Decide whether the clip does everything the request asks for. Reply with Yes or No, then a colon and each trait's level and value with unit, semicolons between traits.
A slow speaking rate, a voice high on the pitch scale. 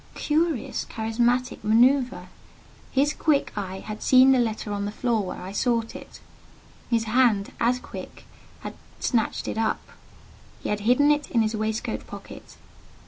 No: average, 150 wpm; high, 230 Hz